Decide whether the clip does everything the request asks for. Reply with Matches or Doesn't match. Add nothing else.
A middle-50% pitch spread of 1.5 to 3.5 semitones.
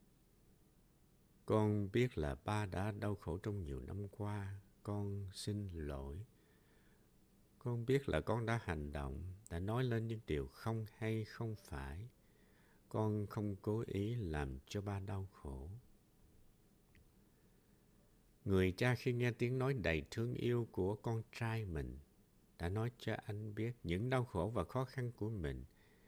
Doesn't match